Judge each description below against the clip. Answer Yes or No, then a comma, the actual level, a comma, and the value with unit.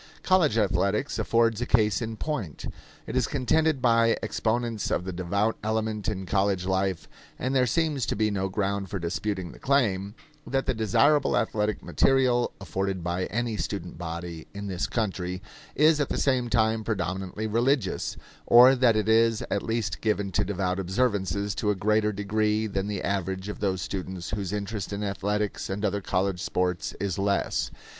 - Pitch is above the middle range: No, low, 105 Hz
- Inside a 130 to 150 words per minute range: No, average, 170 wpm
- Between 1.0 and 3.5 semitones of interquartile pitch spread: Yes, average, 3.2 semitones